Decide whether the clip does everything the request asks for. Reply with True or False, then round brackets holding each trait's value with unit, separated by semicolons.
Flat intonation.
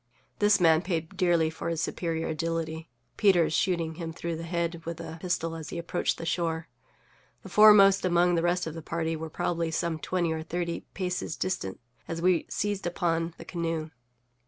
True (1.5 semitones)